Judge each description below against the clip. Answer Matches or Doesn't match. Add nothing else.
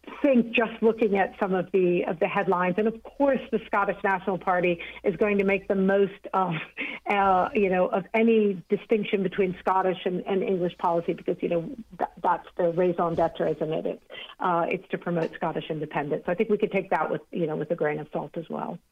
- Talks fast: Matches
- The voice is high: Matches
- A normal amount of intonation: Matches